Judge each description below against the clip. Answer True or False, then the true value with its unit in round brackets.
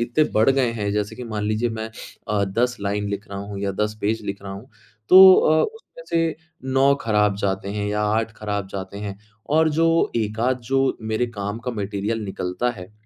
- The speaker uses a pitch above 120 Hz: False (105 Hz)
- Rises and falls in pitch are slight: False (3.7 semitones)